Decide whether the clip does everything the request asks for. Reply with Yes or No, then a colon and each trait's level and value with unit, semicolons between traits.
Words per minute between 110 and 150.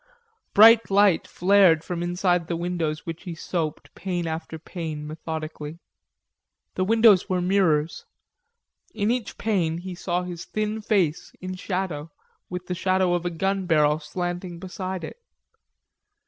Yes: average, 140 wpm